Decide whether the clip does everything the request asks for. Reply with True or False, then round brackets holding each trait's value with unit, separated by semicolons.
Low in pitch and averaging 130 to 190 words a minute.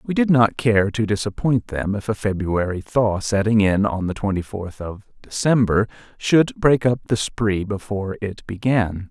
True (105 Hz; 180 wpm)